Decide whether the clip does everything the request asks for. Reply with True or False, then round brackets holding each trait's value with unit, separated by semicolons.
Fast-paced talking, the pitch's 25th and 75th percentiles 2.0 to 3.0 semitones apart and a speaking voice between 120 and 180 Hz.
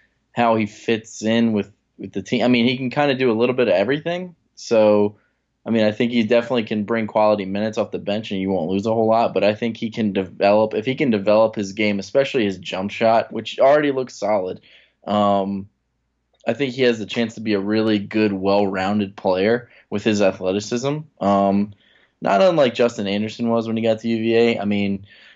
False (220 wpm; 2.5 semitones; 110 Hz)